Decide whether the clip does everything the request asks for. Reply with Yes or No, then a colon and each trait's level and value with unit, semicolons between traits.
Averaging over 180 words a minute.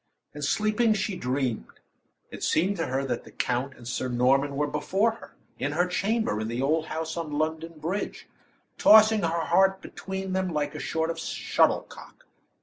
No: average, 175 wpm